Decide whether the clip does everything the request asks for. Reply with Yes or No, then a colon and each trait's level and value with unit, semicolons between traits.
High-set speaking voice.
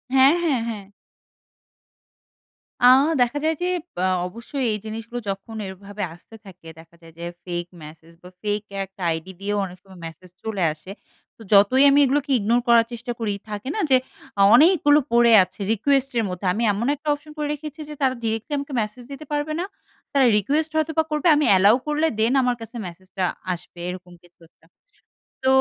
Yes: high, 225 Hz